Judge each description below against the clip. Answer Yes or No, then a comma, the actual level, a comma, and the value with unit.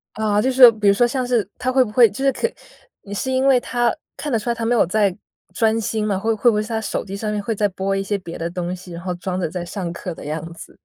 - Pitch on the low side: No, high, 210 Hz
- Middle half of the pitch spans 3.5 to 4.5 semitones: Yes, average, 4.0 semitones